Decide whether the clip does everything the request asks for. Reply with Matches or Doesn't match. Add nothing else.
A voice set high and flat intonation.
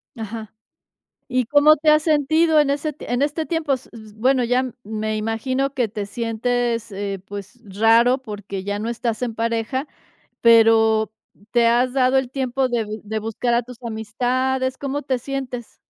Doesn't match